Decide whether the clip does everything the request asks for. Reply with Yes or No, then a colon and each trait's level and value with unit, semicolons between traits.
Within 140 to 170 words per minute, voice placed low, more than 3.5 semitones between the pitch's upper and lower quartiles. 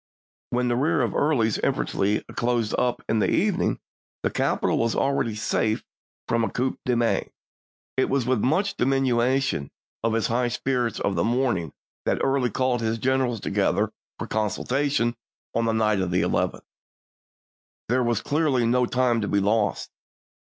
No: average, 165 wpm; low, 120 Hz; average, 2.7 semitones